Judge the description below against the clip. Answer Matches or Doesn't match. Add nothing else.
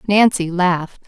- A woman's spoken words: Matches